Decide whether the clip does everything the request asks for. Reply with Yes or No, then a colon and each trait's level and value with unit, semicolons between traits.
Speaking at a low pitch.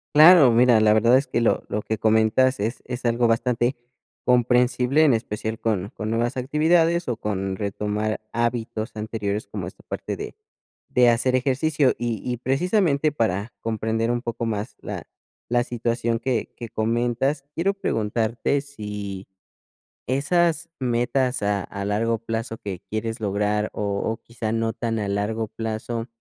Yes: low, 115 Hz